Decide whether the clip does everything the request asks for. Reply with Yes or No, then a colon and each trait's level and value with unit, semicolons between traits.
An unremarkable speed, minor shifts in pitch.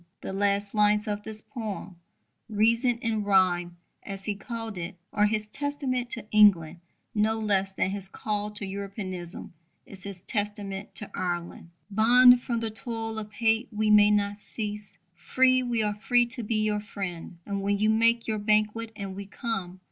Yes: average, 170 wpm; narrow, 2.2 semitones